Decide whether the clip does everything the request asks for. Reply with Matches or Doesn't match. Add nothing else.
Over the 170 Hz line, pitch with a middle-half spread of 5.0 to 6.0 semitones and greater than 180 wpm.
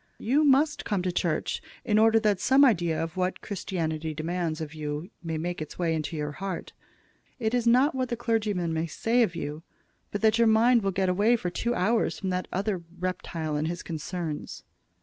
Matches